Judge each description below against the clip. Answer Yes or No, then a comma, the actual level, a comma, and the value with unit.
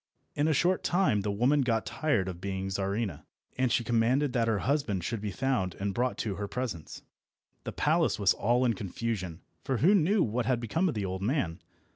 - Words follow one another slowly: No, fast, 205 wpm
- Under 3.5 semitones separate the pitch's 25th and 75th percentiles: No, average, 5.1 semitones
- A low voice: Yes, low, 115 Hz